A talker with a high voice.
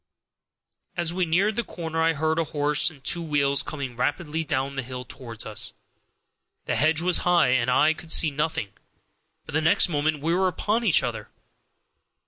No: medium, 155 Hz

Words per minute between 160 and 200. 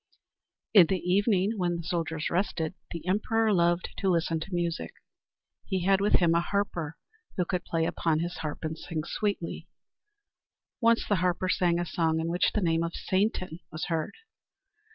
Yes: average, 175 wpm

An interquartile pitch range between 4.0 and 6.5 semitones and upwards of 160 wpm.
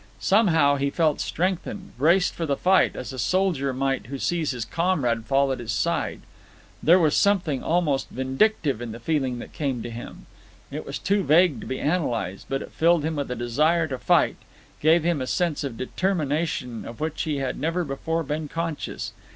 Yes: average, 4.4 semitones; average, 190 wpm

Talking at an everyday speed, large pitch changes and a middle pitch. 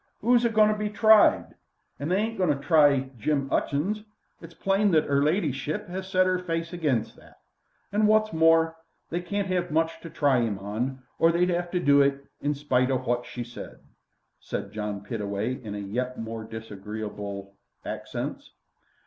Yes: average, 175 wpm; wide, 6.9 semitones; medium, 150 Hz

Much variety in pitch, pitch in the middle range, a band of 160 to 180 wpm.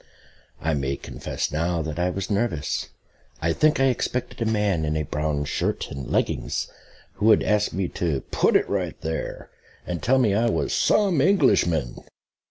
No: wide, 6.5 semitones; very low, 90 Hz; average, 175 wpm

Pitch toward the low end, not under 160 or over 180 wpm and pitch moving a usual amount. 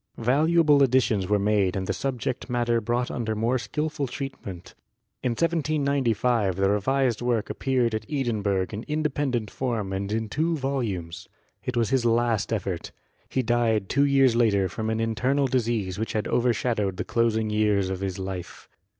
Yes: low, 115 Hz; average, 165 wpm; average, 4.1 semitones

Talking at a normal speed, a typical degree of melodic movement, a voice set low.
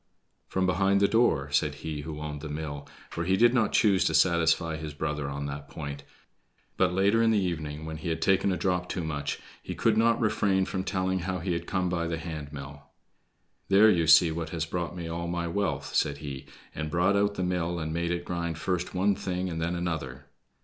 No: fast, 220 wpm; average, 3.3 semitones; very low, 85 Hz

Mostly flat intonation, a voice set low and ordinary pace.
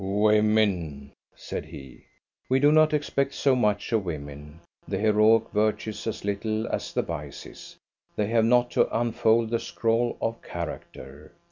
No: average, 4.7 semitones; low, 110 Hz; average, 145 wpm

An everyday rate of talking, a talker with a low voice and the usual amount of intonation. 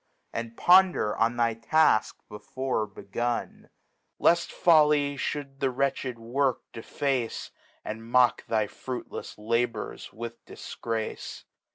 No: slow, 100 wpm; low, 120 Hz; average, 3.3 semitones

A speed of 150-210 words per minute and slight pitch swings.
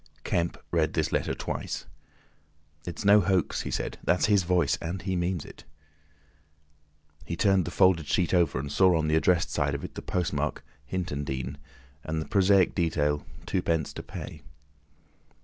No: average, 160 wpm; average, 3.0 semitones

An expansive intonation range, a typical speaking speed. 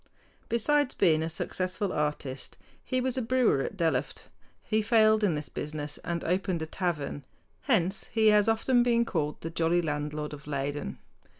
Yes: wide, 6.7 semitones; average, 165 wpm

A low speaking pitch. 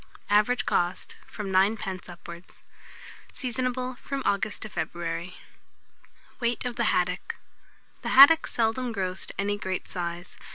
No: high, 205 Hz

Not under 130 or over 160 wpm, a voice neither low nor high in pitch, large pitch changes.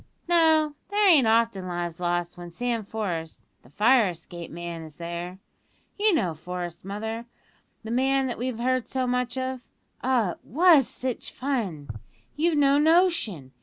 No: average, 155 wpm; high, 230 Hz; wide, 7.3 semitones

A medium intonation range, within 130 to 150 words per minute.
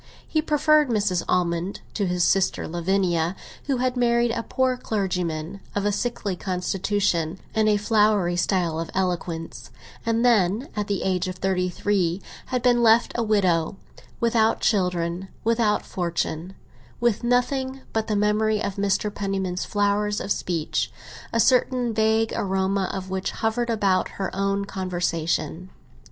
Yes: average, 3.7 semitones; average, 140 wpm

